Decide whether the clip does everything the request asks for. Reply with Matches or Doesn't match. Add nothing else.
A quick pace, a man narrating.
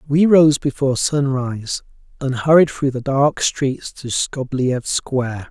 Doesn't match